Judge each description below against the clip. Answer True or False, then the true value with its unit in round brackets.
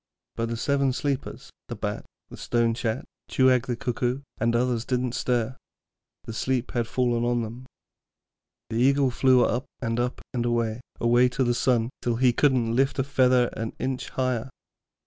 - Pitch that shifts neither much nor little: False (1.7 semitones)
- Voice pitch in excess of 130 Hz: False (125 Hz)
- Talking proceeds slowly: False (175 wpm)